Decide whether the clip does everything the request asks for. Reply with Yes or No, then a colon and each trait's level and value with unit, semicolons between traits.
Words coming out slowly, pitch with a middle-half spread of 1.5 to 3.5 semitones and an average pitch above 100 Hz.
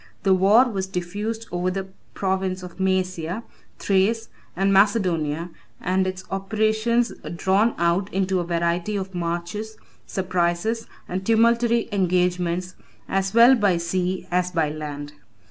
Yes: slow, 130 wpm; average, 2.8 semitones; high, 190 Hz